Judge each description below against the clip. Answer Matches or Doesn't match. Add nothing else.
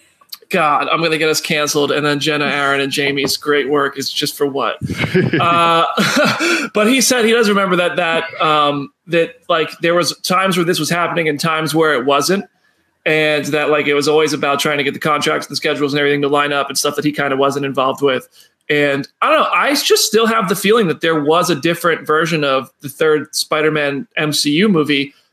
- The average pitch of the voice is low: Doesn't match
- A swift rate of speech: Matches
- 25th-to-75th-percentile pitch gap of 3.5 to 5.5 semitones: Doesn't match